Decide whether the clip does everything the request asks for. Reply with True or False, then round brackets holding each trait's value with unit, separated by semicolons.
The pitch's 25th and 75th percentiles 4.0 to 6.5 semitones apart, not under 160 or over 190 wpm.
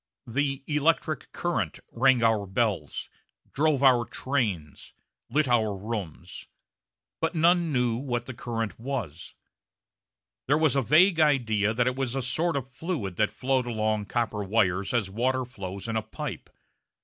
False (4.4 semitones; 150 wpm)